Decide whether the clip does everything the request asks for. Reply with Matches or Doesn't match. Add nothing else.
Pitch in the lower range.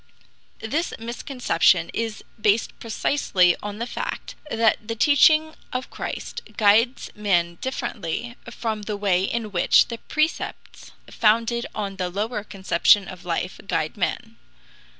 Doesn't match